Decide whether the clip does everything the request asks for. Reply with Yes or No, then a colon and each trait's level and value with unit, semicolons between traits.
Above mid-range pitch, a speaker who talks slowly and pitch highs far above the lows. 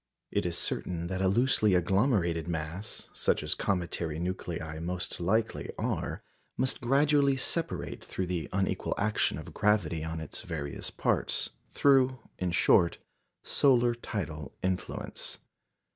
No: very low, 95 Hz; slow, 130 wpm; wide, 6.0 semitones